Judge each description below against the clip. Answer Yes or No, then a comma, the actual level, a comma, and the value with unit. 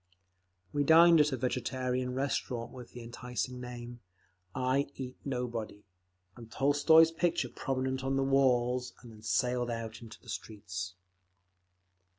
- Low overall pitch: Yes, low, 125 Hz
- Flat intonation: Yes, narrow, 2.2 semitones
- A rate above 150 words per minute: No, slow, 135 wpm